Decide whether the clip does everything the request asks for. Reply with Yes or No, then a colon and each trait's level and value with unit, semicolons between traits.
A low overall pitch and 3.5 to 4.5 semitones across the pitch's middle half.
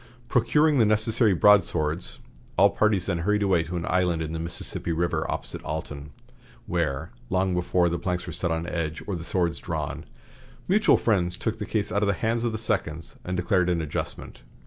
Yes: very low, 90 Hz; average, 3.9 semitones